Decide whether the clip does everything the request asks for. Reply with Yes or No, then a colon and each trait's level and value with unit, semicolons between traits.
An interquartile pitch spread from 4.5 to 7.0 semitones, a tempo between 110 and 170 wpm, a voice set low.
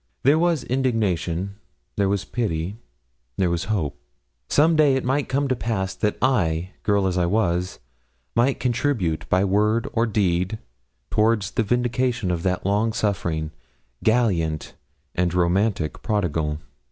Yes: average, 5.1 semitones; average, 140 wpm; low, 100 Hz